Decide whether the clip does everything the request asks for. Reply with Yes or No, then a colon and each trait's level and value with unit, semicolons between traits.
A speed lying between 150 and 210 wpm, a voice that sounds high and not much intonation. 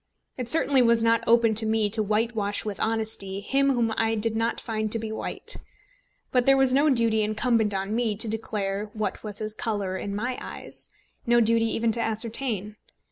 Yes: average, 190 wpm; high, 225 Hz; narrow, 1.6 semitones